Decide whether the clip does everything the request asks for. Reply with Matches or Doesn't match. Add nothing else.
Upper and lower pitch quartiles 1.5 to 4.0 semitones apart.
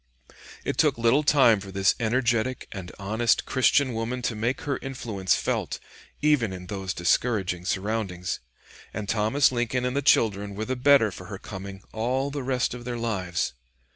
Doesn't match